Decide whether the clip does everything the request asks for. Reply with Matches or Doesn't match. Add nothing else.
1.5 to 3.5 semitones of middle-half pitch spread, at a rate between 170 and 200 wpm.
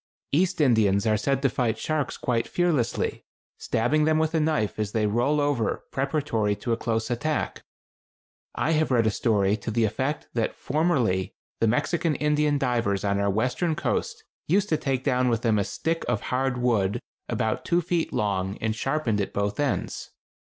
Doesn't match